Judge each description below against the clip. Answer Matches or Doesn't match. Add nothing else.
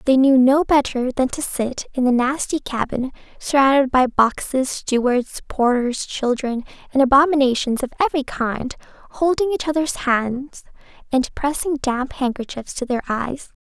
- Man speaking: Doesn't match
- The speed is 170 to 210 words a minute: Doesn't match